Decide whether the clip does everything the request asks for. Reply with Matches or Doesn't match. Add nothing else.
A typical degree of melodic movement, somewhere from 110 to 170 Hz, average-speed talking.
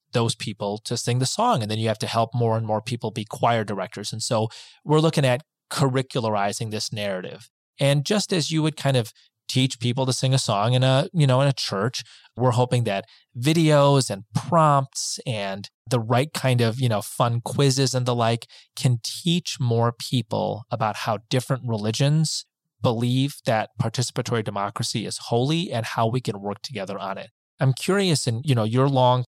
Matches